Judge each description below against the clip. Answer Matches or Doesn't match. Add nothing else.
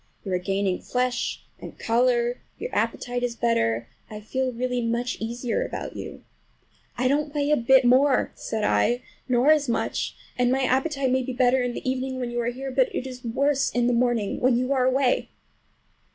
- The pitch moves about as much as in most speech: Doesn't match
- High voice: Matches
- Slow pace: Doesn't match